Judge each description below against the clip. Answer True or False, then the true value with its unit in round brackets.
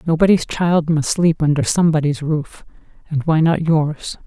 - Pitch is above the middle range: False (155 Hz)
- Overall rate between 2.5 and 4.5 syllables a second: False (4.7 syllables/s)